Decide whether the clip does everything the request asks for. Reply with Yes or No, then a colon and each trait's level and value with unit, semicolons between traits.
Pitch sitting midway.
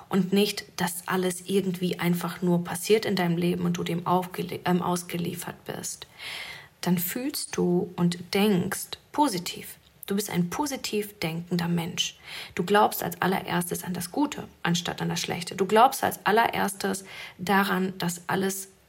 Yes: medium, 180 Hz